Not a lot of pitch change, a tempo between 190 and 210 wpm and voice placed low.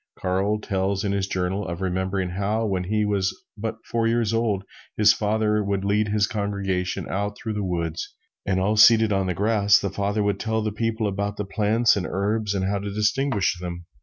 Yes: narrow, 1.9 semitones; average, 200 wpm; low, 100 Hz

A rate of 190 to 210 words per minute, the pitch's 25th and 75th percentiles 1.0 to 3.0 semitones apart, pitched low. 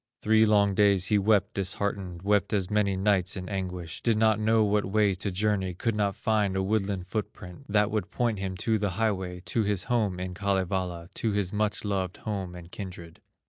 Yes: average, 200 wpm; narrow, 2.4 semitones; low, 100 Hz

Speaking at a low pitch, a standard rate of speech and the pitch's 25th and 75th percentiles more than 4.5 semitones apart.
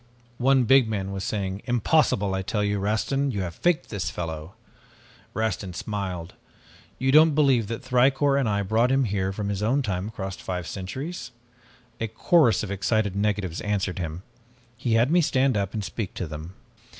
Yes: low, 105 Hz; average, 175 wpm; average, 5.0 semitones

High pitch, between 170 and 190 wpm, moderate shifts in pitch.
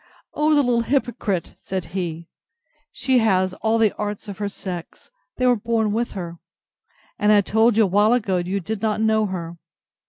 Yes: high, 210 Hz; average, 180 wpm; average, 3.4 semitones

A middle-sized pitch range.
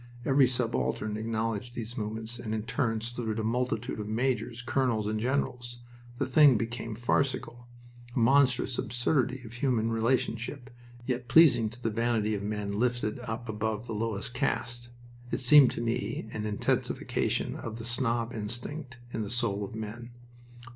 No: narrow, 2.1 semitones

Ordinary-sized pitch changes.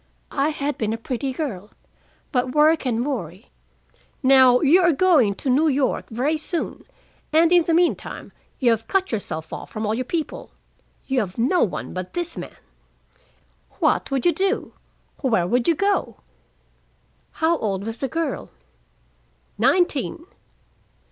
No: wide, 6.2 semitones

